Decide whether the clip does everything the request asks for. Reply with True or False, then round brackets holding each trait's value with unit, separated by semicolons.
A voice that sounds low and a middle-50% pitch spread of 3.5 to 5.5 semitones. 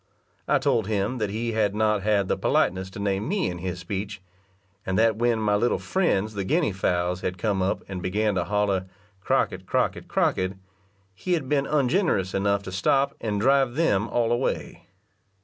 True (105 Hz; 3.9 semitones)